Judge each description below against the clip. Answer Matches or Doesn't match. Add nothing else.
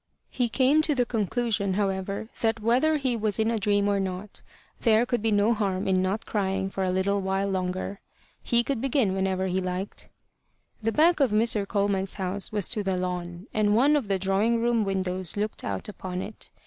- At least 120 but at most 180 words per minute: Doesn't match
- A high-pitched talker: Matches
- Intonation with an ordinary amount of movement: Matches